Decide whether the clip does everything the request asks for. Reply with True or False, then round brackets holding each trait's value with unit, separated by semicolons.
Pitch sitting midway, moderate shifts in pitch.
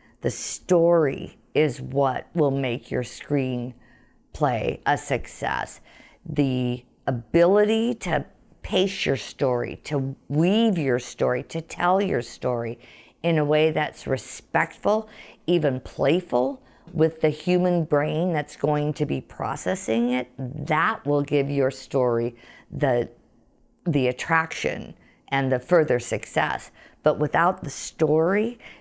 True (145 Hz; 4.7 semitones)